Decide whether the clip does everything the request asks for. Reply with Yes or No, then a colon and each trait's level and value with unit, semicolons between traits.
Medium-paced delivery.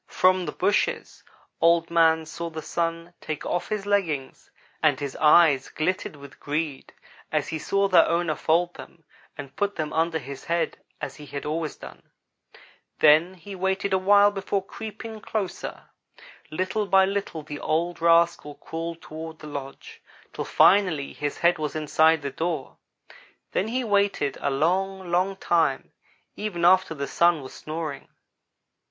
Yes: average, 155 wpm